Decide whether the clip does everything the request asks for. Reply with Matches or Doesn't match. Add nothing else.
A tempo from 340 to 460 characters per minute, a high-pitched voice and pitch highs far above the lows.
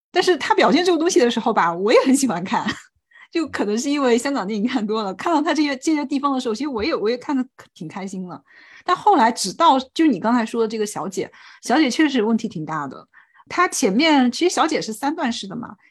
Matches